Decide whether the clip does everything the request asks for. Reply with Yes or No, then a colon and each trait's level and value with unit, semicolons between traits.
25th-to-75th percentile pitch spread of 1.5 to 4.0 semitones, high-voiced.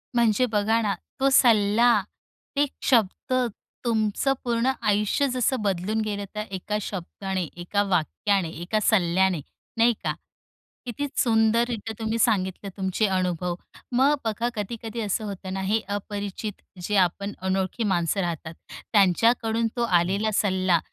Yes: average, 3.3 semitones; high, 210 Hz